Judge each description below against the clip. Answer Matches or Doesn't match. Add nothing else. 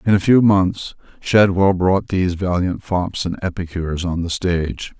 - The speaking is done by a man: Matches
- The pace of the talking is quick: Doesn't match